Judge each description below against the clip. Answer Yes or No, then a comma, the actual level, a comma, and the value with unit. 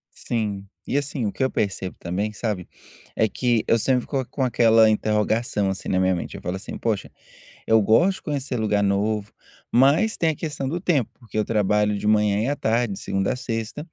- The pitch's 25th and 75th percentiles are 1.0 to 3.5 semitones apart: No, average, 3.9 semitones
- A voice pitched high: No, low, 110 Hz